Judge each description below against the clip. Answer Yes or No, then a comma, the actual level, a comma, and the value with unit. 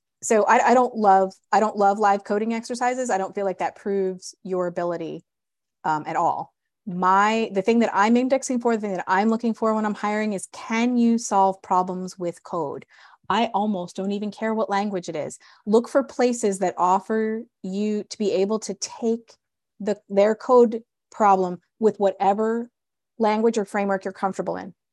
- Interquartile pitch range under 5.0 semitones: Yes, average, 2.9 semitones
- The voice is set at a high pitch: Yes, high, 205 Hz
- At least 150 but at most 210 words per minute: Yes, average, 185 wpm